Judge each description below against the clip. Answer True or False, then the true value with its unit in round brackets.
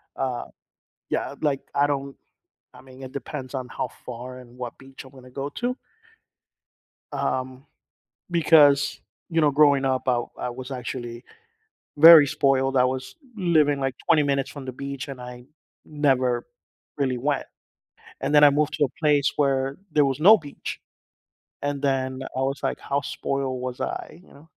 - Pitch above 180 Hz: False (135 Hz)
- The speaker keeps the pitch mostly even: True (2.0 semitones)